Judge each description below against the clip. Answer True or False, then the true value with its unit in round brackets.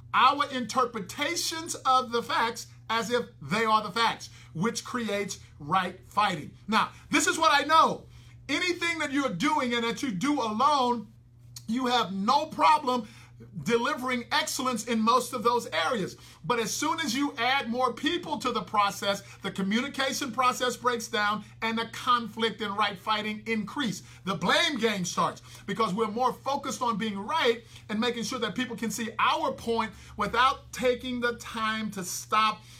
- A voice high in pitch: True (235 Hz)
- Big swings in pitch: False (3.5 semitones)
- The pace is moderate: True (165 wpm)